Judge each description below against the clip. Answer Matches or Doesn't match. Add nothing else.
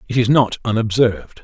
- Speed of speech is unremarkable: Matches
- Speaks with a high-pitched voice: Doesn't match